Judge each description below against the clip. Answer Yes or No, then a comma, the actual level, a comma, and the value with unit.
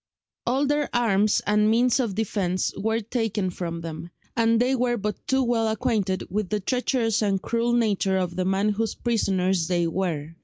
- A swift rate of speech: No, average, 180 wpm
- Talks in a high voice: Yes, high, 210 Hz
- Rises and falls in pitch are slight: No, average, 3.9 semitones